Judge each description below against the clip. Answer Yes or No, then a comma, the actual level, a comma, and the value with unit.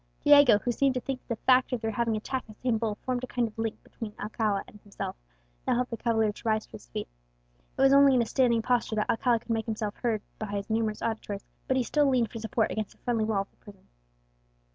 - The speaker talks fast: Yes, fast, 255 wpm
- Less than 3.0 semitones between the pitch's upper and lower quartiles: Yes, narrow, 2.6 semitones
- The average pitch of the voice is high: Yes, high, 225 Hz